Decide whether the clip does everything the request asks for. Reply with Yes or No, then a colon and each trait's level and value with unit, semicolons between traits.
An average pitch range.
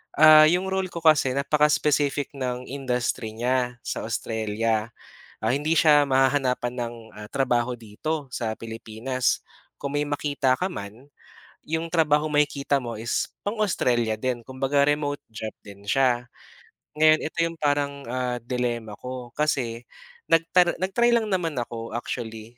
Yes: average, 4.0 semitones